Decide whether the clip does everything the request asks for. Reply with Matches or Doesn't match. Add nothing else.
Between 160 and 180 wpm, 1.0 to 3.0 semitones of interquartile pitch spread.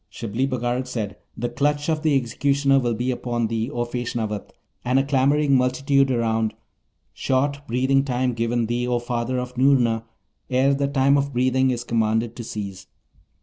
Matches